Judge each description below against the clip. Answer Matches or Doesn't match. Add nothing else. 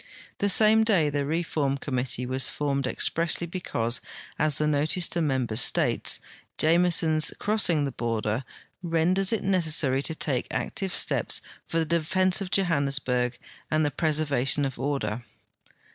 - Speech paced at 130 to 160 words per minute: Matches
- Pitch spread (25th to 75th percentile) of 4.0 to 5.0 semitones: Matches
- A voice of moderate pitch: Matches